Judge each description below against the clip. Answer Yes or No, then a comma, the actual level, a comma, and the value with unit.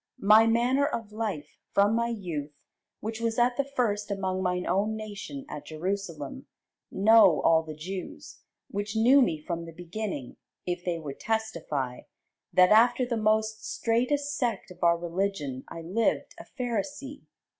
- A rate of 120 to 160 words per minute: Yes, average, 155 wpm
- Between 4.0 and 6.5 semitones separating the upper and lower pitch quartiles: Yes, average, 5.2 semitones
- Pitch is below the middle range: No, high, 205 Hz